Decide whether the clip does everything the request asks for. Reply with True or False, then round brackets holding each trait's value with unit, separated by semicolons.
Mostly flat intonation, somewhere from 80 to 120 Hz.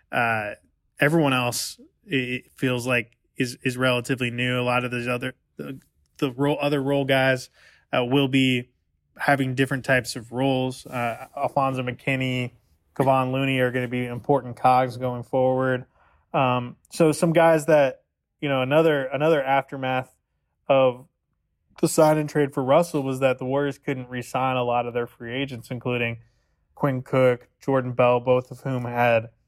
False (1.8 semitones; 130 Hz)